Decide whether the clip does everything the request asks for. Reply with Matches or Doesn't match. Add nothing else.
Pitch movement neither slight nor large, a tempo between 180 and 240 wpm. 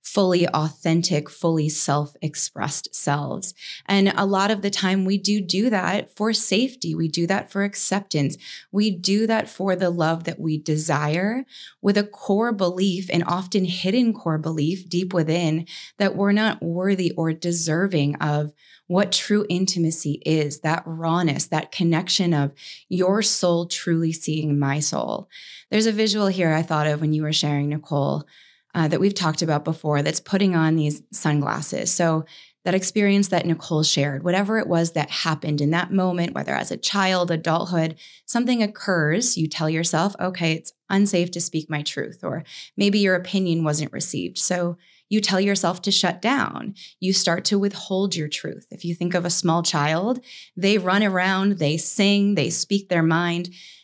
Doesn't match